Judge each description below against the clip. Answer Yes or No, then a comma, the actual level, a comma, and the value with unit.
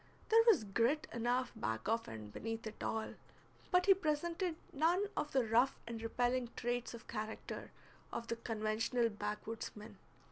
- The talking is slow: No, average, 155 wpm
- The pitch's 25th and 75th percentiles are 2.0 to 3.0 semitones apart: No, average, 4.9 semitones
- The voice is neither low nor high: No, high, 235 Hz